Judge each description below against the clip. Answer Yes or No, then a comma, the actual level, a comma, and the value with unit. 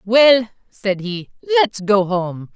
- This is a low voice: No, high, 215 Hz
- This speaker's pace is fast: No, average, 140 wpm